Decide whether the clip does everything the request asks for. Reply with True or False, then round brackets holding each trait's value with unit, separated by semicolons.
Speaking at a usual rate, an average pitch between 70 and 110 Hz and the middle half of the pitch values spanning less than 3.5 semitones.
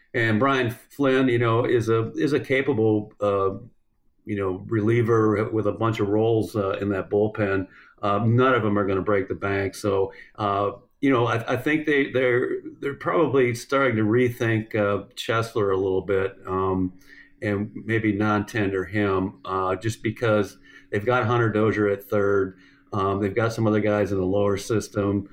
True (180 wpm; 105 Hz; 2.8 semitones)